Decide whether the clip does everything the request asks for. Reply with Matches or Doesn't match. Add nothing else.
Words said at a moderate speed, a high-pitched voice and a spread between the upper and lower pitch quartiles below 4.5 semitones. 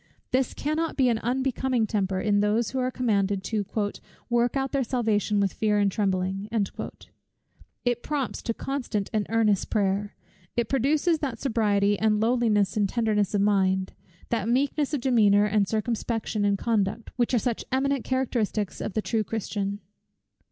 Matches